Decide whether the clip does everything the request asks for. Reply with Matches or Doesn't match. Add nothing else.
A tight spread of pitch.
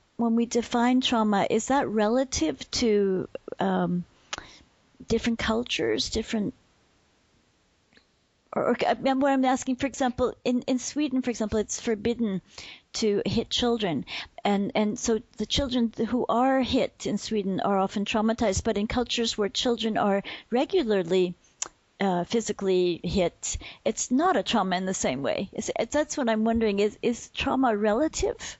Doesn't match